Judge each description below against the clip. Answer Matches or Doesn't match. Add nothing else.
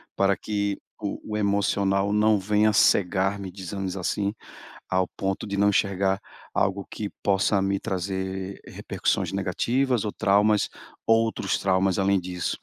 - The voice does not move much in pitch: Matches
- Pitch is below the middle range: Matches